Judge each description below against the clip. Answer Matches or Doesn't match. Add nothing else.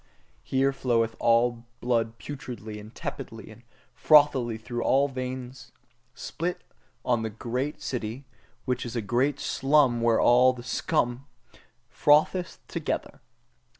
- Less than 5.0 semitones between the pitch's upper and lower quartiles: Matches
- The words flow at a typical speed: Doesn't match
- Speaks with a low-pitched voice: Matches